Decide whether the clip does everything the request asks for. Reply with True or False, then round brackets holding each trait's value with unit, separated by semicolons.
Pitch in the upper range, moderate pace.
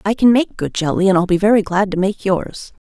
False (195 Hz; 270 wpm)